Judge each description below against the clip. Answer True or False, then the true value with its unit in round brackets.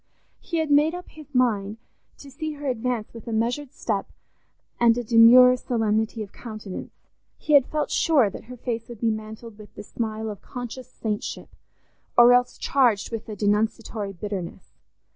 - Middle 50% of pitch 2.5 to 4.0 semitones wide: True (2.8 semitones)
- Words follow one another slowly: False (165 wpm)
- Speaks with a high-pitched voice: True (230 Hz)